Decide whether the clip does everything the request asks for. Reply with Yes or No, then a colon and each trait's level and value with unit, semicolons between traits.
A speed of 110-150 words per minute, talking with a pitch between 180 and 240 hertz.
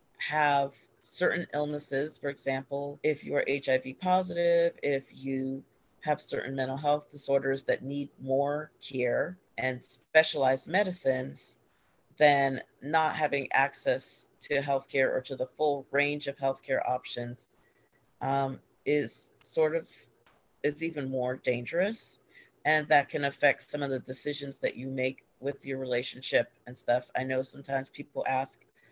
No: average, 140 wpm; medium, 140 Hz